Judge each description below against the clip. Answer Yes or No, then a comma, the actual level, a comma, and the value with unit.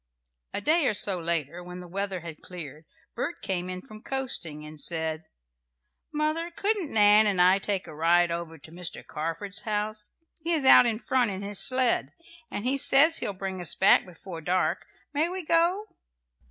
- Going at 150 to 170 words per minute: No, average, 180 wpm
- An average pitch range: No, wide, 7.3 semitones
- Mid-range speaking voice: No, high, 195 Hz